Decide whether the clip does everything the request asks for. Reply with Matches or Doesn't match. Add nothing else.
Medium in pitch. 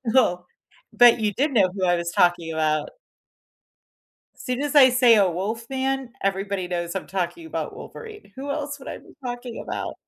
Doesn't match